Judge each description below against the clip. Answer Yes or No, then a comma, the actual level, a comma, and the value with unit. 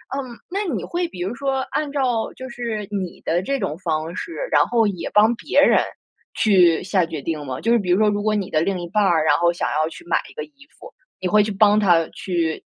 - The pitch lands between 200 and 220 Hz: Yes, high, 205 Hz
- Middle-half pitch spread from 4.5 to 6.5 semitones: Yes, wide, 5.6 semitones